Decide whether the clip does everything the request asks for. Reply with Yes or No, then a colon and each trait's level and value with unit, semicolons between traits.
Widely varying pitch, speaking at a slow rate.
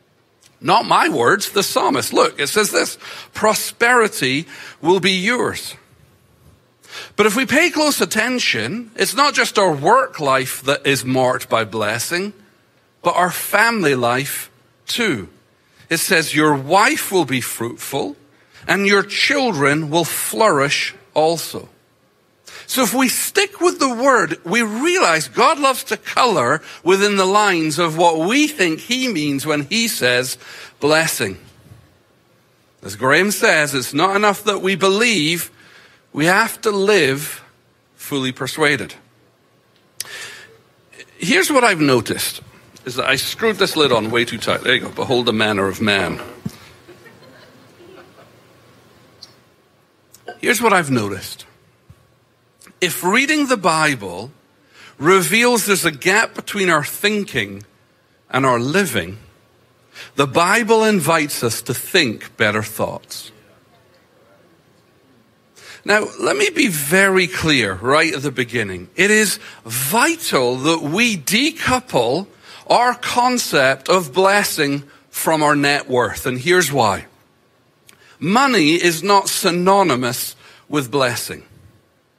Yes: wide, 8.6 semitones; slow, 125 wpm